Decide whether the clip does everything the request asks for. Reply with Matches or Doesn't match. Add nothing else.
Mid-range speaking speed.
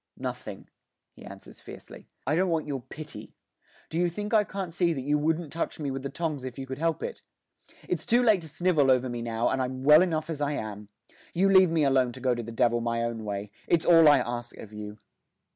Doesn't match